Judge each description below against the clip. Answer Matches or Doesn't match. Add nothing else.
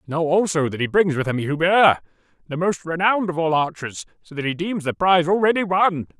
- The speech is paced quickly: Matches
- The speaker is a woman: Doesn't match